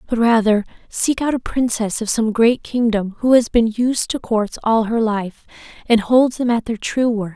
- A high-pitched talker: Yes, high, 225 Hz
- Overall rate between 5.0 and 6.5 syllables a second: No, 4.5 syllables/s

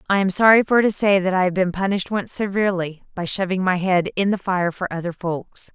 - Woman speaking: Yes, female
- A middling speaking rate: No, fast, 240 wpm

